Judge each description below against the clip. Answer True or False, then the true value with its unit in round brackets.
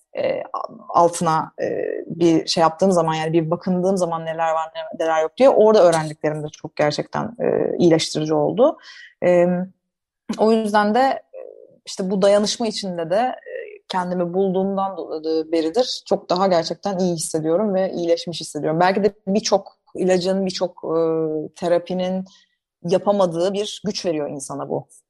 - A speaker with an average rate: True (125 wpm)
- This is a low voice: False (185 Hz)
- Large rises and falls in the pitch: False (4.0 semitones)